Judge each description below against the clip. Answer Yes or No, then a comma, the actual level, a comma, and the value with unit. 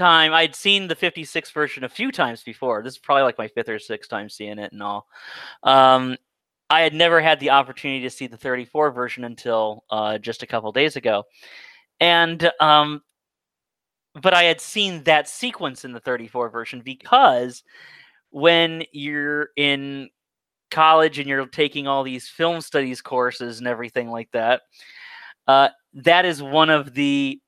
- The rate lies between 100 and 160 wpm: No, average, 170 wpm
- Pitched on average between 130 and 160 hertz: Yes, medium, 140 Hz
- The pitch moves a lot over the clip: No, average, 4.6 semitones